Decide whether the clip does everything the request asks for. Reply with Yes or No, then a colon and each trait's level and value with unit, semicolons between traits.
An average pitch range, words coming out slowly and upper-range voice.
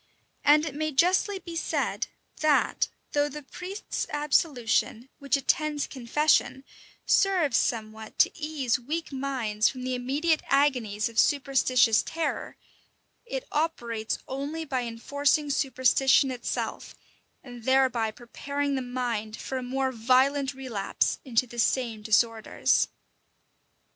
Yes: average, 3.7 semitones; slow, 120 wpm; very high, 265 Hz